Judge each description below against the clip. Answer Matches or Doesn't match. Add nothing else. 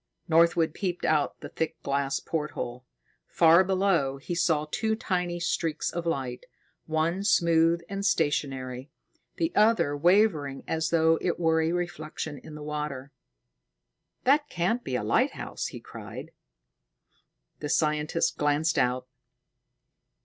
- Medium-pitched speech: Matches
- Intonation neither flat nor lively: Matches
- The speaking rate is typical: Doesn't match